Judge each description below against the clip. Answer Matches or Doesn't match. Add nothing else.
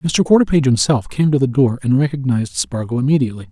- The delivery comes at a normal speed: Matches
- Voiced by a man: Matches